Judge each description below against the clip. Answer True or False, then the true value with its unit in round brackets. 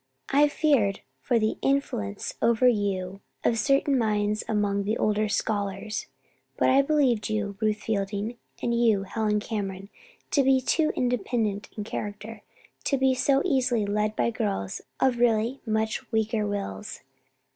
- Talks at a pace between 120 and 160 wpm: True (145 wpm)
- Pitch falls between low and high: False (215 Hz)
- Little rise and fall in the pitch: False (3.2 semitones)